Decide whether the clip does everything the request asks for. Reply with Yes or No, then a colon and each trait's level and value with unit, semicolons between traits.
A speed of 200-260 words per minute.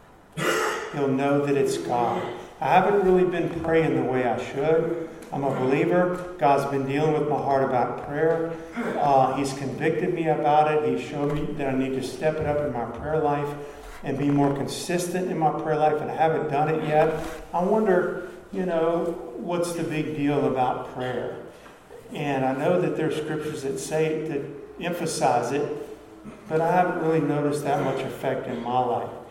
No: average, 190 wpm